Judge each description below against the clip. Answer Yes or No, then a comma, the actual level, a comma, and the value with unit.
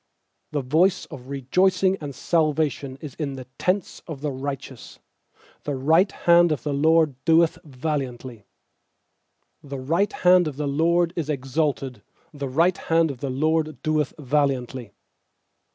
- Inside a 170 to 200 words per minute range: No, average, 140 wpm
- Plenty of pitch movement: No, average, 3.4 semitones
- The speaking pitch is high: No, medium, 150 Hz